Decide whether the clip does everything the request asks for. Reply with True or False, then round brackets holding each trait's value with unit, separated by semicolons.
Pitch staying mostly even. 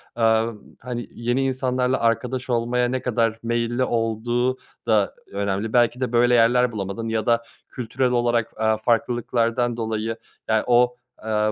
True (1.7 semitones)